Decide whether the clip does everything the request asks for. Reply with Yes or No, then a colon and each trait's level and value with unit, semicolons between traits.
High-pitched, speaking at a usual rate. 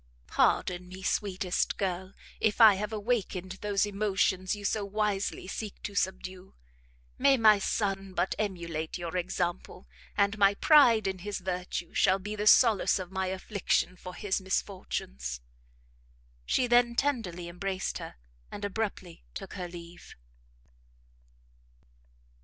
No: high, 195 Hz; slow, 130 wpm